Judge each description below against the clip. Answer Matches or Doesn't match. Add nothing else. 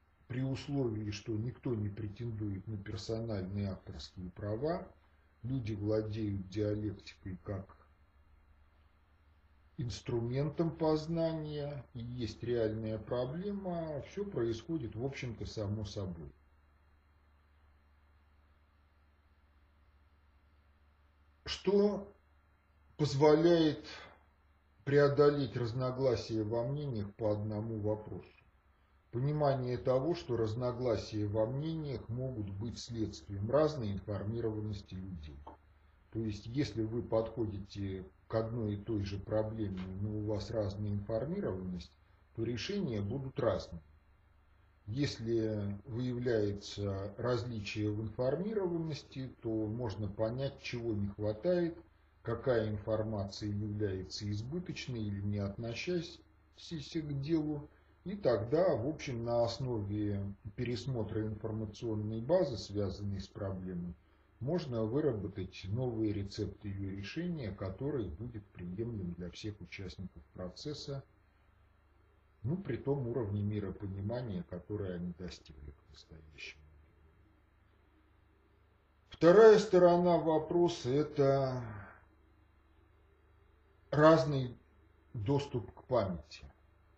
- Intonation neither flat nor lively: Doesn't match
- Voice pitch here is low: Matches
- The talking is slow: Matches